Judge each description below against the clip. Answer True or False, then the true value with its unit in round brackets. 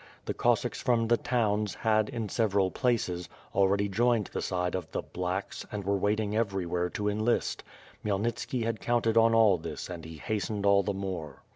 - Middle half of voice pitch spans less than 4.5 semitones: True (3.2 semitones)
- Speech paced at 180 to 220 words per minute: True (185 wpm)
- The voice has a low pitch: True (105 Hz)